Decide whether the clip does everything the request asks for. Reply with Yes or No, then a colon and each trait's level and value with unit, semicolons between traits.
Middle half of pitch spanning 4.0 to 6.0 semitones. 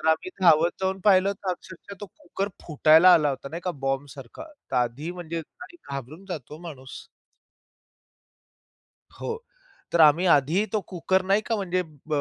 Yes: average, 4.5 semitones